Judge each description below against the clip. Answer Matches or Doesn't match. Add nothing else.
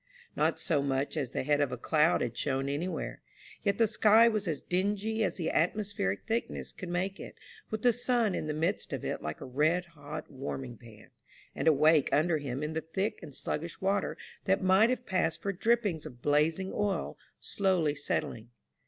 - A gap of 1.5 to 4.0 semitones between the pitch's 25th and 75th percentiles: Doesn't match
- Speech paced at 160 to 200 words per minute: Matches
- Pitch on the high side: Doesn't match